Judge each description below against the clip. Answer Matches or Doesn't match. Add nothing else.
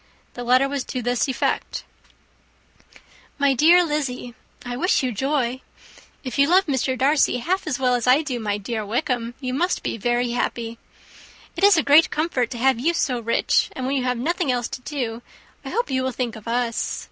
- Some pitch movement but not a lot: Matches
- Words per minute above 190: Matches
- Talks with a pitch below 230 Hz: Doesn't match